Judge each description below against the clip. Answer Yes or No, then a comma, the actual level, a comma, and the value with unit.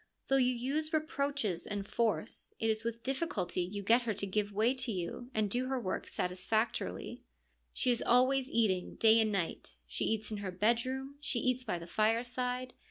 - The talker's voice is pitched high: Yes, high, 230 Hz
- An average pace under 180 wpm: No, average, 190 wpm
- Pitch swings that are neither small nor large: Yes, average, 3.9 semitones